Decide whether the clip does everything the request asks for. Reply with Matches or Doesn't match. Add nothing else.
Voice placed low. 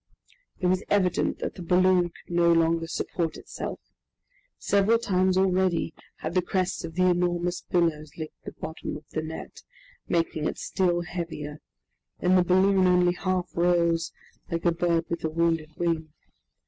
Doesn't match